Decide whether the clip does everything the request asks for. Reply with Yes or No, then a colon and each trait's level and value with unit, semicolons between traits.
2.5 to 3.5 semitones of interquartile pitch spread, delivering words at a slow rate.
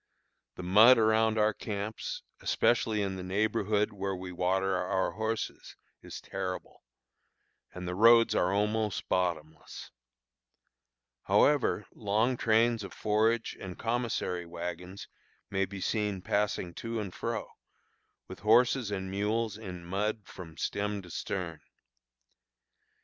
Yes: average, 3.1 semitones; slow, 120 wpm